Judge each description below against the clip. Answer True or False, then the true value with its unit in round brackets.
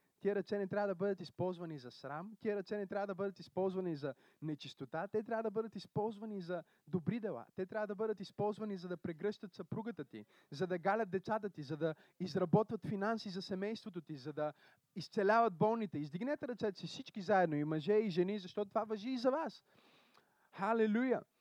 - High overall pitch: True (200 Hz)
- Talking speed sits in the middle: False (190 wpm)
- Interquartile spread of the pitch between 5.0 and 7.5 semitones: False (3.6 semitones)